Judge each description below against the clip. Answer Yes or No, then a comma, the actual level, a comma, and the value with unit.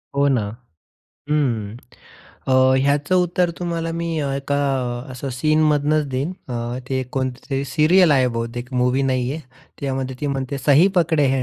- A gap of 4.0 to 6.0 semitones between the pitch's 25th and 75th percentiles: No, average, 3.1 semitones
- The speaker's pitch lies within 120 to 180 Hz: Yes, medium, 140 Hz